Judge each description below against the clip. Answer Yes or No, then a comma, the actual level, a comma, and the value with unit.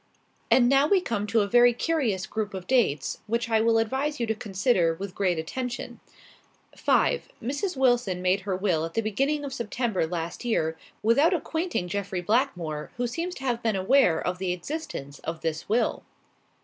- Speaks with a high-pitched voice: Yes, high, 220 Hz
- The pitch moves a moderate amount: No, wide, 6.3 semitones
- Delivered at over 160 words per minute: Yes, average, 180 wpm